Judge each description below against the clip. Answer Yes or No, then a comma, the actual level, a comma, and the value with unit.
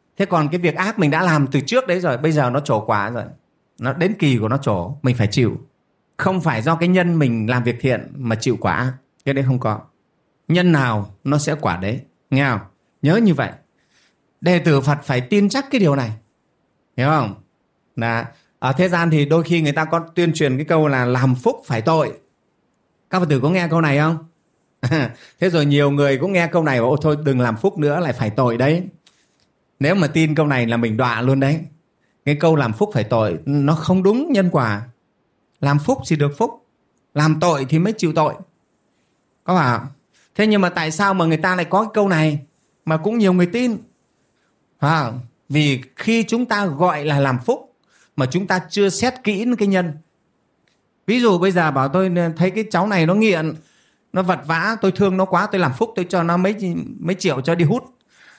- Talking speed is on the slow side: No, average, 220 wpm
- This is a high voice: No, medium, 160 Hz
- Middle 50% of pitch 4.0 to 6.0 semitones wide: Yes, average, 5.2 semitones